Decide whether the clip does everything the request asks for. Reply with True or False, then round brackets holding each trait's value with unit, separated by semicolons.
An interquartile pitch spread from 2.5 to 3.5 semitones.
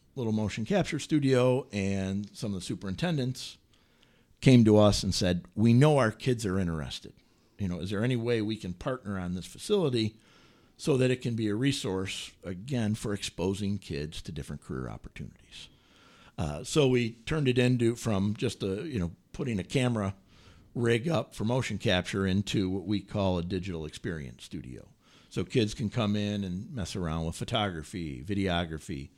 False (4.5 semitones)